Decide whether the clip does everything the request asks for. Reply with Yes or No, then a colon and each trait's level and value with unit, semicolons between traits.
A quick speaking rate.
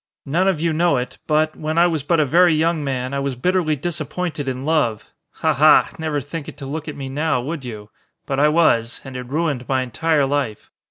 Yes: fast, 225 wpm